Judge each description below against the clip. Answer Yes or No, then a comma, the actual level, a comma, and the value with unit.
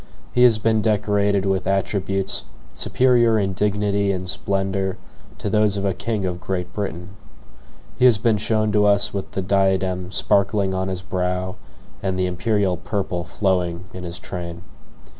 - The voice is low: Yes, very low, 95 Hz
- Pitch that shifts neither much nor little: No, narrow, 1.9 semitones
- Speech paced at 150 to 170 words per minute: Yes, average, 160 wpm